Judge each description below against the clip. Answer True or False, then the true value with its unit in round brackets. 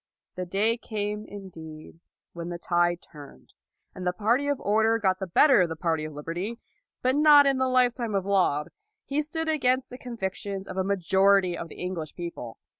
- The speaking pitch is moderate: False (195 Hz)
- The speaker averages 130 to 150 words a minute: False (190 wpm)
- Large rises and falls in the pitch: True (5.8 semitones)